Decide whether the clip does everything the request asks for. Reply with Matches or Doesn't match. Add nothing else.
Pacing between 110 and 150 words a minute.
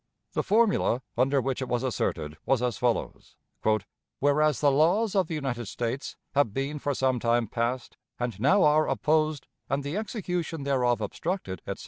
Doesn't match